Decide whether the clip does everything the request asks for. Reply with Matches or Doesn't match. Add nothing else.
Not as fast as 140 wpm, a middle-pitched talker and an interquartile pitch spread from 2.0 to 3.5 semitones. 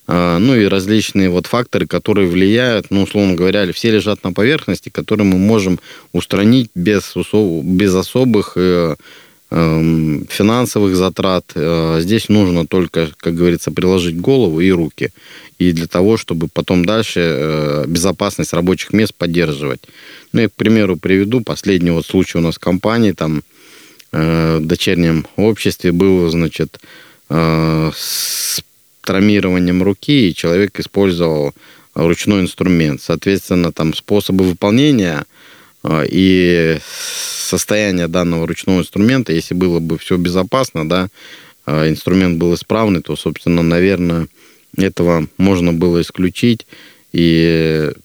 Doesn't match